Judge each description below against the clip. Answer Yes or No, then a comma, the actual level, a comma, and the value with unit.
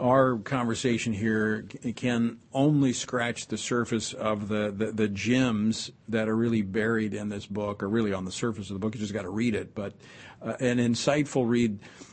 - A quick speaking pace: No, average, 195 wpm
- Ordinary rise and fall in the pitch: No, narrow, 2.3 semitones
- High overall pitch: No, low, 115 Hz